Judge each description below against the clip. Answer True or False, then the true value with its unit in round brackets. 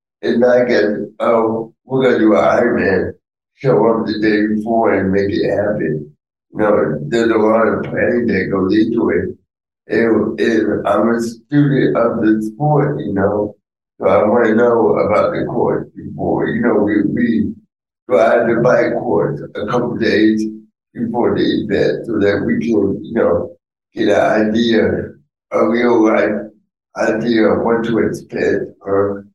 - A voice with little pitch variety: True (1.8 semitones)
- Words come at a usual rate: True (165 wpm)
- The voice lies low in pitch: True (110 Hz)